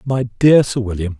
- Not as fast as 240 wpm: Yes, average, 200 wpm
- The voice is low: Yes, low, 115 Hz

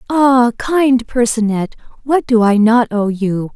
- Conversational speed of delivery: Yes, average, 150 wpm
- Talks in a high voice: Yes, high, 235 Hz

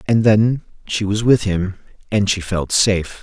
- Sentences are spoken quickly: No, average, 185 wpm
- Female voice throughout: No, male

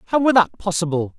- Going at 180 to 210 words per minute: Yes, average, 200 wpm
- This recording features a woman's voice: No, male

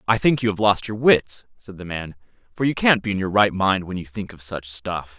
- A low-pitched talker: Yes, low, 100 Hz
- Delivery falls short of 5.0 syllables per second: No, 5.2 syllables/s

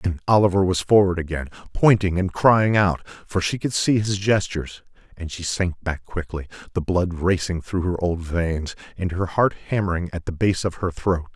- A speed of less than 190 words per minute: No, average, 195 wpm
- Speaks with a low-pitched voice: Yes, very low, 90 Hz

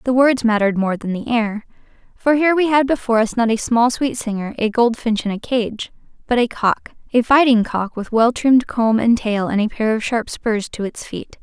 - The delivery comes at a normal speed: No, fast, 225 wpm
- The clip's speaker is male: No, female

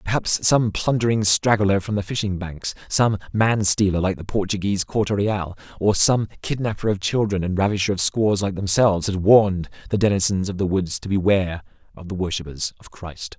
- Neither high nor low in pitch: No, low, 100 Hz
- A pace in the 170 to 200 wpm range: Yes, average, 175 wpm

